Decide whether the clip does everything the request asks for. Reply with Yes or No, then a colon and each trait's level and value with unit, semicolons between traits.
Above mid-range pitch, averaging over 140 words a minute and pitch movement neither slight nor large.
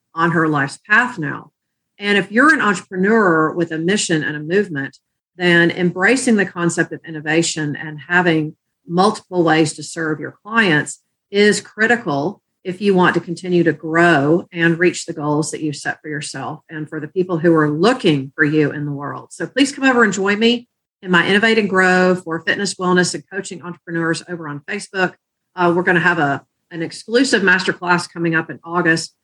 No: medium, 175 Hz; average, 195 wpm; average, 3.5 semitones